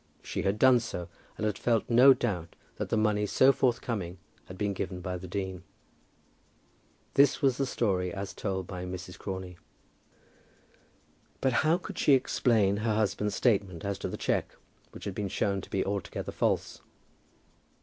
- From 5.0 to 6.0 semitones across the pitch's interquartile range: No, average, 4.0 semitones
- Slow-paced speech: No, average, 165 wpm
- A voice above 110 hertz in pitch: No, low, 100 Hz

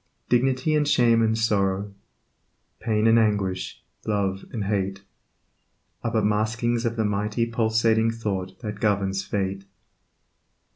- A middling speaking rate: No, slow, 125 wpm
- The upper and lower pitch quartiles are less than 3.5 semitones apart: Yes, narrow, 2.5 semitones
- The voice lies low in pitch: Yes, low, 110 Hz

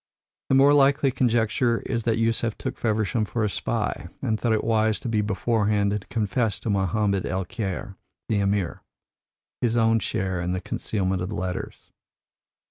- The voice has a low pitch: Yes, low, 110 Hz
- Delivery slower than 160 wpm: No, average, 175 wpm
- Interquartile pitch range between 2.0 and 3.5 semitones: Yes, average, 2.7 semitones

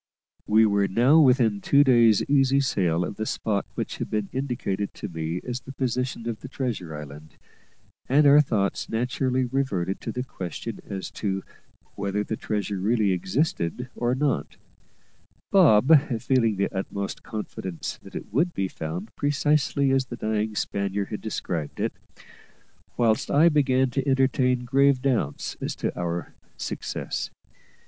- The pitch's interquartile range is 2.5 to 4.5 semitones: No, average, 5.1 semitones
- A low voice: Yes, low, 115 Hz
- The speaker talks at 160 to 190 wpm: No, average, 150 wpm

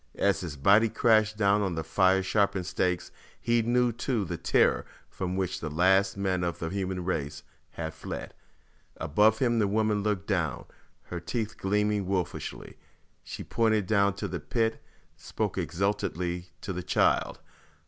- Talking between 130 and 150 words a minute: No, average, 160 wpm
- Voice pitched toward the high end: No, very low, 95 Hz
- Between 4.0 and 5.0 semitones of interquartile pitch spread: No, average, 3.1 semitones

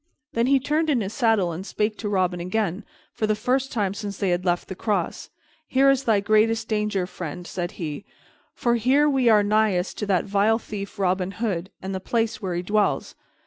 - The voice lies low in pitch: No, high, 210 Hz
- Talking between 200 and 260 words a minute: Yes, fast, 205 wpm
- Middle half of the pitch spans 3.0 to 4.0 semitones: Yes, average, 3.4 semitones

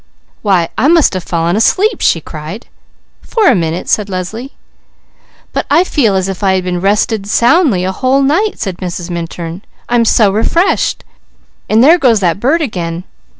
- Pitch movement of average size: No, wide, 7.0 semitones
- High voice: Yes, high, 205 Hz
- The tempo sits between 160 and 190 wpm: Yes, average, 165 wpm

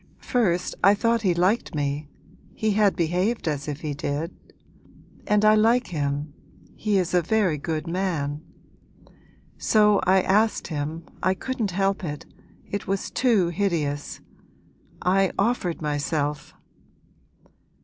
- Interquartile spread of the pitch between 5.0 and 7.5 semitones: Yes, average, 5.3 semitones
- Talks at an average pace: No, slow, 130 wpm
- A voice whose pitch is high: No, medium, 180 Hz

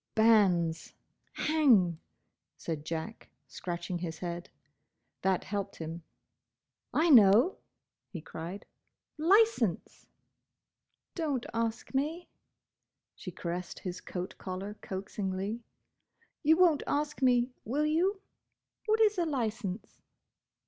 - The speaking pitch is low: No, high, 215 Hz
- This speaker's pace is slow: Yes, slow, 100 wpm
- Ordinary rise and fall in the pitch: No, wide, 8.9 semitones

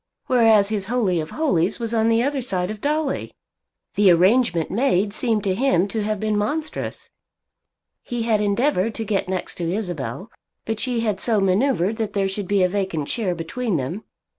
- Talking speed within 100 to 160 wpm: No, average, 185 wpm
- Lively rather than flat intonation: No, average, 3.7 semitones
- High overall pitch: Yes, high, 210 Hz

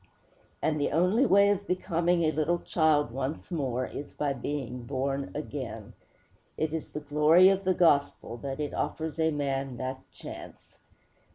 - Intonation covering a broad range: No, average, 3.8 semitones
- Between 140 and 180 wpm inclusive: Yes, average, 160 wpm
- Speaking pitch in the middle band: Yes, medium, 150 Hz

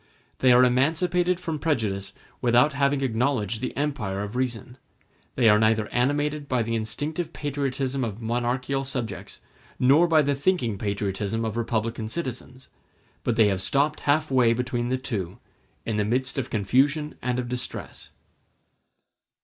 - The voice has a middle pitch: No, low, 125 Hz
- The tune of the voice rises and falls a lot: No, average, 4.0 semitones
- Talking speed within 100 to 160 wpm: Yes, average, 145 wpm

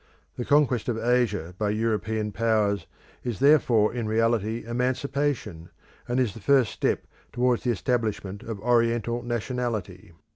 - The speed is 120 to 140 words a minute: Yes, slow, 135 wpm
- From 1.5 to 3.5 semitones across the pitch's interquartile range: Yes, narrow, 2.6 semitones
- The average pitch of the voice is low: Yes, low, 115 Hz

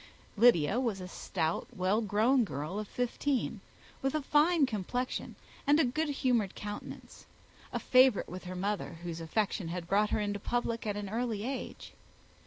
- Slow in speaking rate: No, average, 160 wpm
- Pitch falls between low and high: No, high, 215 Hz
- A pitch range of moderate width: Yes, average, 4.9 semitones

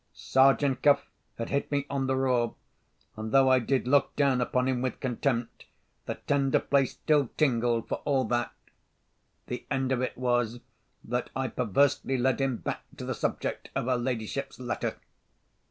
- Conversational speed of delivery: Yes, average, 170 wpm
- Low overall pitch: Yes, low, 130 Hz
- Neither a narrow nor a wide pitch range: No, narrow, 2.0 semitones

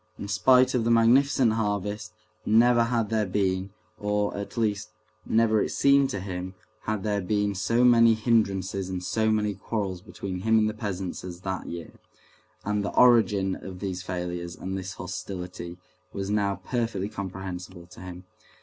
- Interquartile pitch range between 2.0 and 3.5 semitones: Yes, average, 3.1 semitones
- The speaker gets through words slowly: No, average, 165 wpm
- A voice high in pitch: No, low, 100 Hz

